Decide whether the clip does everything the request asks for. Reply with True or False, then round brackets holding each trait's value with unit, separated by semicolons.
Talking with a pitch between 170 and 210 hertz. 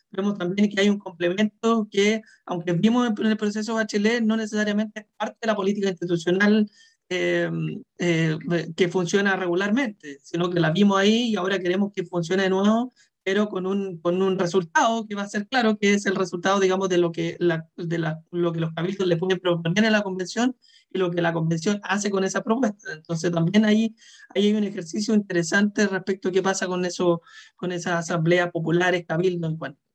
True (190 Hz)